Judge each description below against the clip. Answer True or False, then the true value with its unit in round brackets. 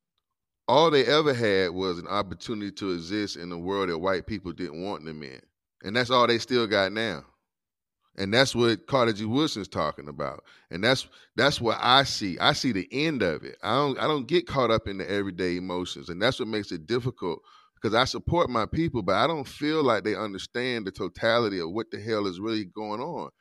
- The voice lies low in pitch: True (105 Hz)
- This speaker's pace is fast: True (220 wpm)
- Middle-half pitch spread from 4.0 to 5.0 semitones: True (4.5 semitones)